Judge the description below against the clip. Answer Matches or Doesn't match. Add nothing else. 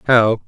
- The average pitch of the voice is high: Doesn't match